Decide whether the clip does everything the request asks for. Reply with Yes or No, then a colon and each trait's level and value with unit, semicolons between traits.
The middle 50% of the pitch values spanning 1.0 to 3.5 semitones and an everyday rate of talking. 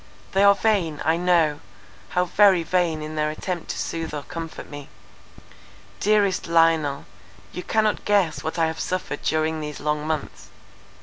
Yes: average, 3.0 semitones; average, 160 wpm